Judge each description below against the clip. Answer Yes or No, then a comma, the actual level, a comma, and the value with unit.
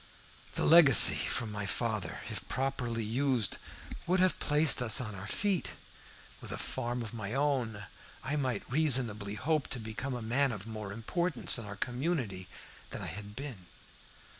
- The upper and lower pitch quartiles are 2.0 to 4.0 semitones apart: No, average, 4.6 semitones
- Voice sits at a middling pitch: No, low, 120 Hz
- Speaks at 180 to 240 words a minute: No, average, 165 wpm